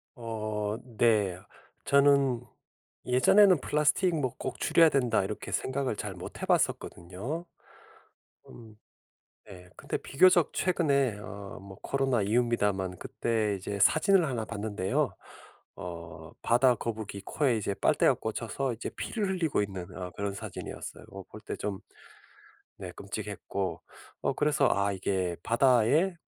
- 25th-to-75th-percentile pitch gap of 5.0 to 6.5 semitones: Yes, wide, 5.6 semitones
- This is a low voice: Yes, low, 115 Hz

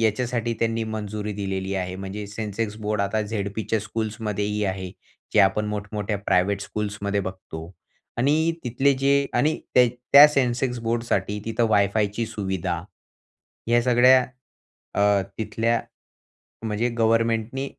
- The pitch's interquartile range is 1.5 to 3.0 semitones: Yes, narrow, 2.6 semitones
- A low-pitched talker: Yes, low, 110 Hz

